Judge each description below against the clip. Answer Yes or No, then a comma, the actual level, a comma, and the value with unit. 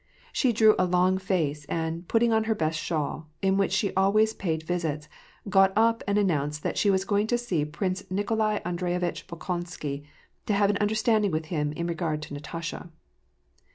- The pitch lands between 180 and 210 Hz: Yes, medium, 185 Hz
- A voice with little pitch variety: No, average, 4.3 semitones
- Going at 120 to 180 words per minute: No, average, 190 wpm